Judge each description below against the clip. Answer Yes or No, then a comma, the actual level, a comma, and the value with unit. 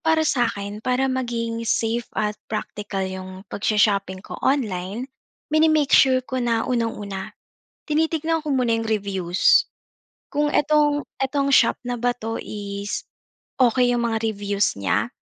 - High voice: Yes, high, 230 Hz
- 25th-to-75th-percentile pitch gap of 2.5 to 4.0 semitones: No, average, 4.5 semitones